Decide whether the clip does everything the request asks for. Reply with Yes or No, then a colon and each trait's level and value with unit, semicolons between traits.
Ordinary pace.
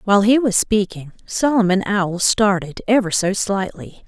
Yes: average, 145 wpm